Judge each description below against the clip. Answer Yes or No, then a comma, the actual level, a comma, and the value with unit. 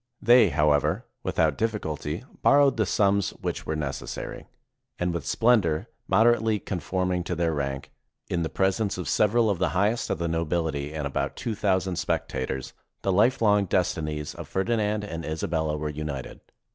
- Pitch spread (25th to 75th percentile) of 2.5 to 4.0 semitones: No, average, 5.2 semitones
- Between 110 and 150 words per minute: No, average, 160 wpm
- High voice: No, very low, 90 Hz